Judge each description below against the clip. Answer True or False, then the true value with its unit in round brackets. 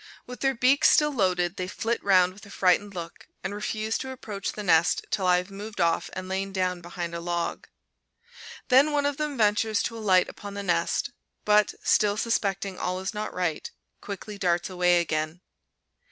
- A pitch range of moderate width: True (3.2 semitones)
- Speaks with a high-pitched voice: True (195 Hz)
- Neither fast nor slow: True (185 wpm)